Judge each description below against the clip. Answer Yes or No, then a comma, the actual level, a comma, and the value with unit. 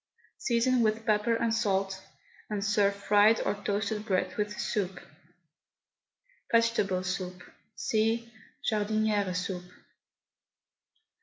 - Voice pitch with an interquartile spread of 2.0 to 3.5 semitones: Yes, narrow, 2.5 semitones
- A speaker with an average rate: No, slow, 100 wpm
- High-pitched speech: Yes, high, 210 Hz